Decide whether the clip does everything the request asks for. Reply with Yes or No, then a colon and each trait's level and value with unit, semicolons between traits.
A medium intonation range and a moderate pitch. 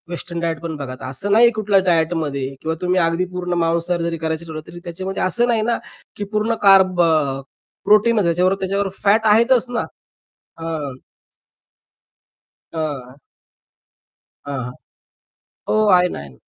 Yes: average, 3.7 semitones; medium, 175 Hz